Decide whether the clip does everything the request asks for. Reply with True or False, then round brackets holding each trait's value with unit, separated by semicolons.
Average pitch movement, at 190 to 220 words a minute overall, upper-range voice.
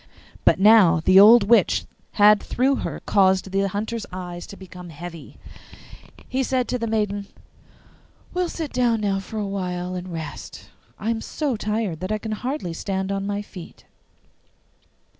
False (3.5 semitones; 165 wpm; 200 Hz)